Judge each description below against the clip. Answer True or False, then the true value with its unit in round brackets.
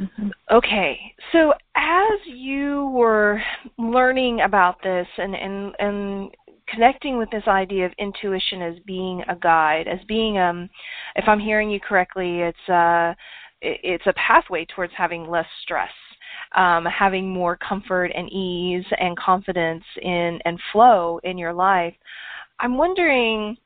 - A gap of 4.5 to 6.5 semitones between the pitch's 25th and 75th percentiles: False (4.0 semitones)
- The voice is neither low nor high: False (195 Hz)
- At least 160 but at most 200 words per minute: False (135 wpm)